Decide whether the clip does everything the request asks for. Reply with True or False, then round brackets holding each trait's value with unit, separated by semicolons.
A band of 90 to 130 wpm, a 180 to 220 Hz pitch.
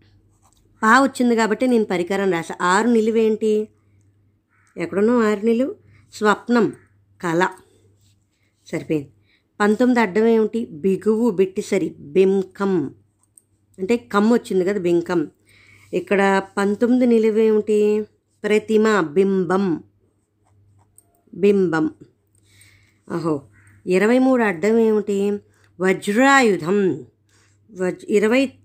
False (80 wpm; 190 Hz)